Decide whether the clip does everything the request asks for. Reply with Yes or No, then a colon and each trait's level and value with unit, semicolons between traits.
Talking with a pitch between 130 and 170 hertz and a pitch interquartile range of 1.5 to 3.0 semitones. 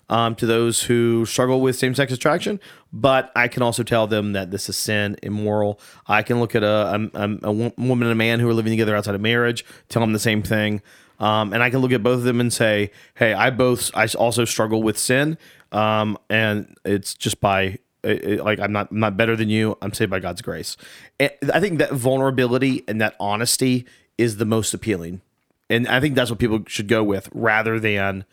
No: low, 115 Hz; narrow, 2.6 semitones